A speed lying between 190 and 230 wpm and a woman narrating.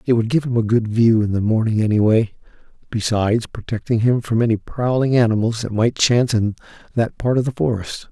No: average, 200 wpm; male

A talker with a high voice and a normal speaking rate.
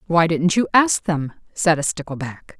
No: medium, 165 Hz; average, 185 wpm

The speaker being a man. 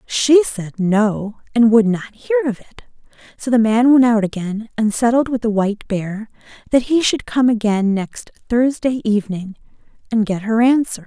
No: female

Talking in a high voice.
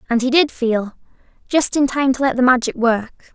Yes: very high, 255 Hz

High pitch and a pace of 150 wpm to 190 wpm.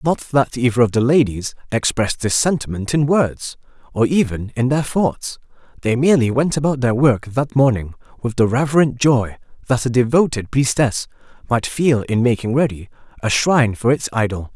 No: low, 125 Hz; average, 175 wpm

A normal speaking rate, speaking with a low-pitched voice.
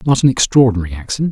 Yes: average, 180 wpm; low, 120 Hz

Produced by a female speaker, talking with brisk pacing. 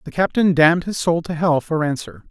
No: male; fast, 235 wpm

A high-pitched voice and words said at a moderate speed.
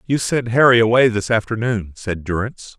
No: low, 110 Hz; average, 175 wpm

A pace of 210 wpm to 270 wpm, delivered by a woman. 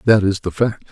No: fast, 265 wpm; male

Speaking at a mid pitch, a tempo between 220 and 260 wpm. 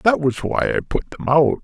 Yes: medium, 145 Hz; fast, 255 wpm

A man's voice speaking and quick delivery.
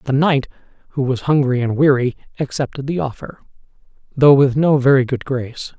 No: male; average, 165 wpm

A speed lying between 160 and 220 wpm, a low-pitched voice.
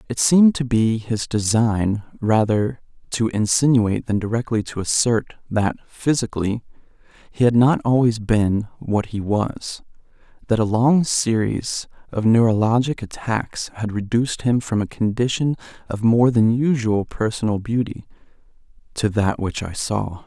No: slow, 135 wpm; low, 115 Hz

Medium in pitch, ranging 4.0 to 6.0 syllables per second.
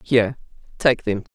Yes: medium, 175 Hz; 5.1 syllables/s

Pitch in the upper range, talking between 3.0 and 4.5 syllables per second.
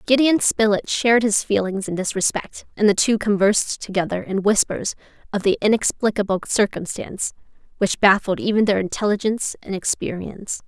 No: high, 205 Hz; 5.5 syllables/s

